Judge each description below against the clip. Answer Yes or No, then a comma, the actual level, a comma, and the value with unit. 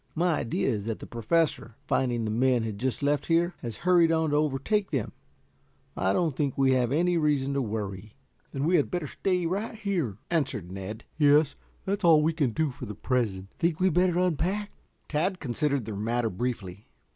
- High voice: No, medium, 140 Hz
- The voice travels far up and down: Yes, wide, 6.6 semitones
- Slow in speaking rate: No, average, 200 wpm